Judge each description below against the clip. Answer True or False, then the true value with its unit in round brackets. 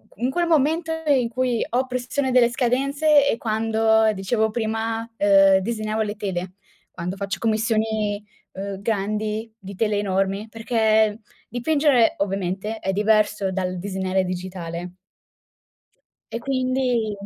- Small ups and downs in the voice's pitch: False (3.5 semitones)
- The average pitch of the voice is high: True (220 Hz)